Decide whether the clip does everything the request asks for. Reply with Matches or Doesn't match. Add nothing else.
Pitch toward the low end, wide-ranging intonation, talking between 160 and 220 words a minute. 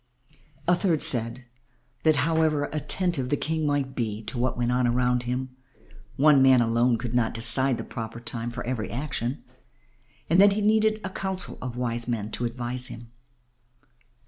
Doesn't match